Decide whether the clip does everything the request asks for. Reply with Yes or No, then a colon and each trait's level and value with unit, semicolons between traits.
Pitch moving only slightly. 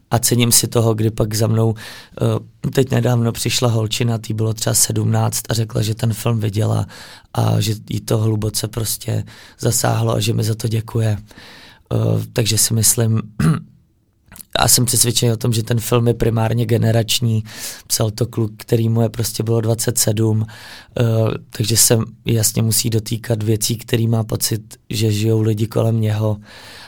Yes: narrow, 1.2 semitones